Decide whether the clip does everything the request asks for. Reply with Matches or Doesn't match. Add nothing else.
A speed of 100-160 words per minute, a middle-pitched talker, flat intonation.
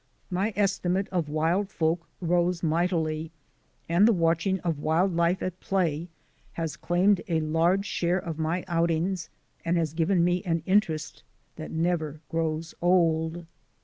Matches